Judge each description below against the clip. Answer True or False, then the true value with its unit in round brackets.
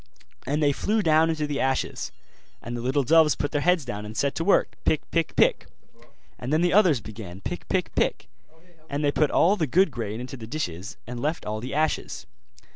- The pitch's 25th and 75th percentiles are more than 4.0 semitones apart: True (4.9 semitones)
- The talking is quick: True (210 wpm)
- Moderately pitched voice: True (145 Hz)